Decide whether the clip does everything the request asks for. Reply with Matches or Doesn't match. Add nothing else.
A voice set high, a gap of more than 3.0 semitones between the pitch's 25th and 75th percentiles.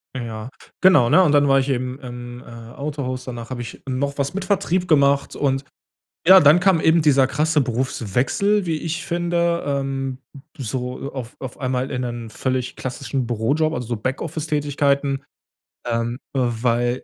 Doesn't match